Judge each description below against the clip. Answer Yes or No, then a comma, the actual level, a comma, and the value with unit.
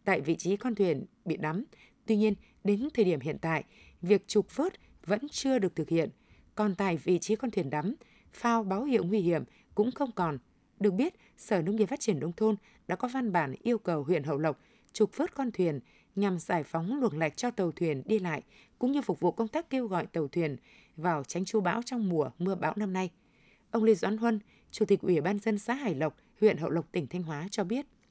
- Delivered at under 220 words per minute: No, average, 235 wpm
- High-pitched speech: Yes, high, 200 Hz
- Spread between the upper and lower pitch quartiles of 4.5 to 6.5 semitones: Yes, average, 4.8 semitones